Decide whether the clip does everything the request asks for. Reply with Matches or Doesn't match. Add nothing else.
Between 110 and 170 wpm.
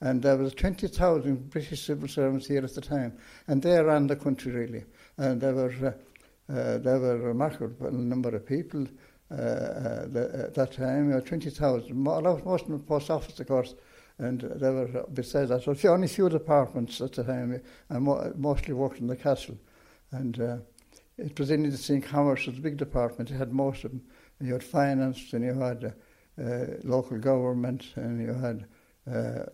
Doesn't match